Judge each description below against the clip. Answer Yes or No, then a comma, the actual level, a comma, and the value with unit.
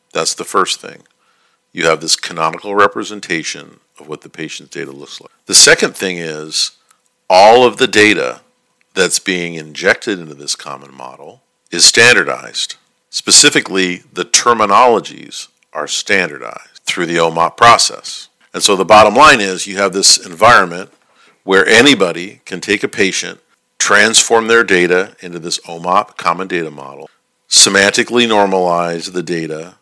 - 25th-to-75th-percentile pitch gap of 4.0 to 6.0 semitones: No, average, 3.5 semitones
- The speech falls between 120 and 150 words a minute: Yes, average, 145 wpm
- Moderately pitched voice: No, very low, 90 Hz